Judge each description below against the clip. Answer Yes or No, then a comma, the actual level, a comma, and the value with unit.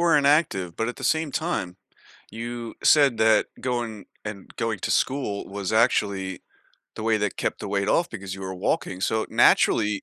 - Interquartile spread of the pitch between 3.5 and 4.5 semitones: Yes, average, 3.9 semitones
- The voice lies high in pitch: No, low, 110 Hz